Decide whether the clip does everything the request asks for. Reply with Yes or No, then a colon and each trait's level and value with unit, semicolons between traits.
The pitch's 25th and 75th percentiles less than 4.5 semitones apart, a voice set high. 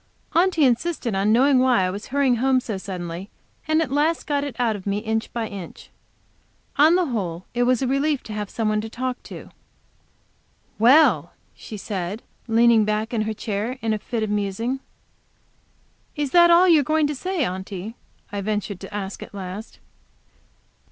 No: average, 5.2 semitones; high, 225 Hz